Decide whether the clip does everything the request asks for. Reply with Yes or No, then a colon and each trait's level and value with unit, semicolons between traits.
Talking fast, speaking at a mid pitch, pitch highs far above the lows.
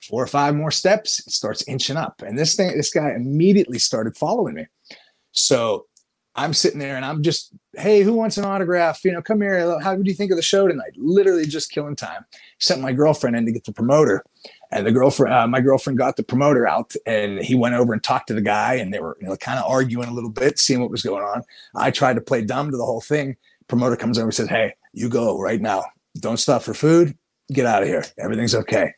Yes: fast, 245 wpm; medium, 145 Hz; wide, 6.2 semitones